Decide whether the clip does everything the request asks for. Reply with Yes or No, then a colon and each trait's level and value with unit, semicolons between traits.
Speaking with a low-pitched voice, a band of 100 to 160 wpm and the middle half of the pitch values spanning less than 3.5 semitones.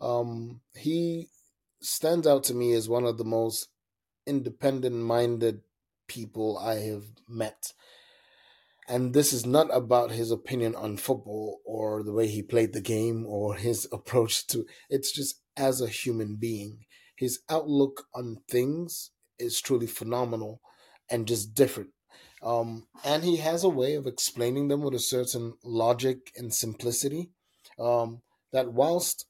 Yes: low, 120 Hz; average, 145 wpm; average, 3.1 semitones